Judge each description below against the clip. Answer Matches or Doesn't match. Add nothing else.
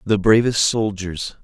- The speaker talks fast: Doesn't match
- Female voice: Doesn't match